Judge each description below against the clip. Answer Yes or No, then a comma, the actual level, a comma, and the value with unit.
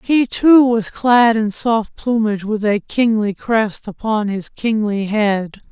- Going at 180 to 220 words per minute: No, average, 160 wpm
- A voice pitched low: No, high, 220 Hz